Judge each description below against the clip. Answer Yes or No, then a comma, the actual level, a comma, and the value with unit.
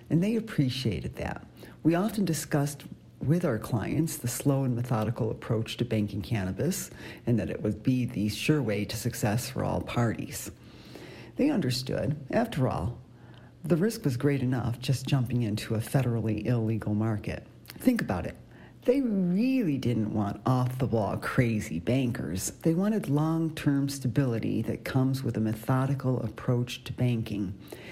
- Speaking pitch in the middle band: No, low, 125 Hz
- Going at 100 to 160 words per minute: Yes, average, 155 wpm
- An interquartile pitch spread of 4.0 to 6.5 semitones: Yes, average, 4.4 semitones